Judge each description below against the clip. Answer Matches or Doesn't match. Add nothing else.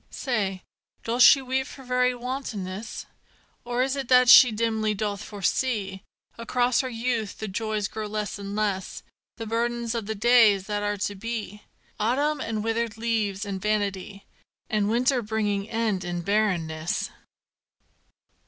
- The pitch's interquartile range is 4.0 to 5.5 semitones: Doesn't match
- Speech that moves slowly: Doesn't match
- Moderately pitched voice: Doesn't match